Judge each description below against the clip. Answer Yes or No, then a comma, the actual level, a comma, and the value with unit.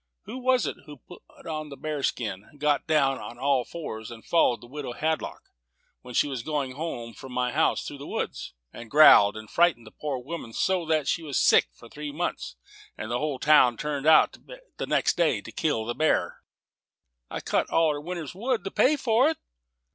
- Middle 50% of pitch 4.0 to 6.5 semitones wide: Yes, average, 4.5 semitones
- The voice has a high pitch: No, medium, 150 Hz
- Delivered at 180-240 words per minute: Yes, average, 200 wpm